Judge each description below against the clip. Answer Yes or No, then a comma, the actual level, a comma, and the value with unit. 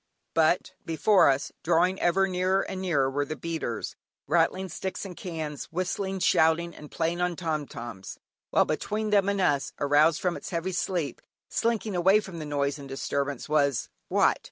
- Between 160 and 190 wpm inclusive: Yes, average, 170 wpm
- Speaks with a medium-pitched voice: Yes, medium, 165 Hz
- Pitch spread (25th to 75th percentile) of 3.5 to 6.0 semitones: Yes, average, 4.3 semitones